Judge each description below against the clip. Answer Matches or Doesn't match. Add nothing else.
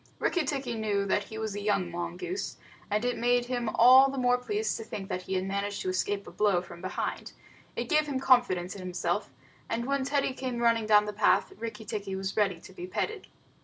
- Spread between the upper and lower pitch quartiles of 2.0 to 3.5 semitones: Doesn't match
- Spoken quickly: Matches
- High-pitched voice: Matches